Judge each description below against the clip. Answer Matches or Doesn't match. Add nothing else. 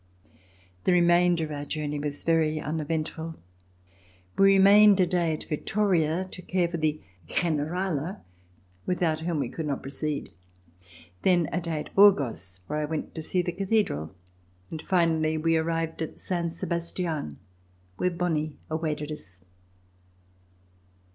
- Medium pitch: Matches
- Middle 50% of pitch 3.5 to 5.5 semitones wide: Doesn't match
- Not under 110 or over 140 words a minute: Matches